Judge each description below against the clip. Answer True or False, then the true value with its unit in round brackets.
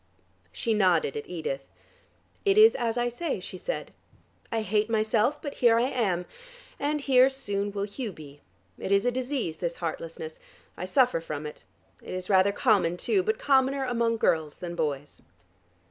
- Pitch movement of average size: False (6.9 semitones)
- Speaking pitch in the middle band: False (215 Hz)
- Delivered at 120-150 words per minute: False (170 wpm)